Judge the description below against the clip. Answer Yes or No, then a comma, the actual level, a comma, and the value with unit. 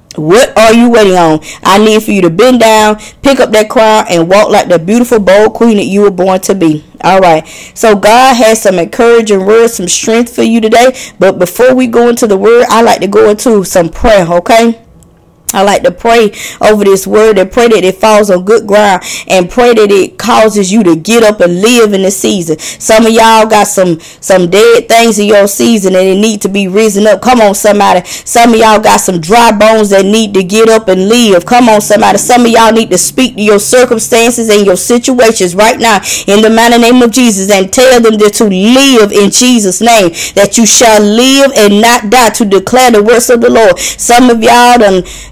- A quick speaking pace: Yes, fast, 225 wpm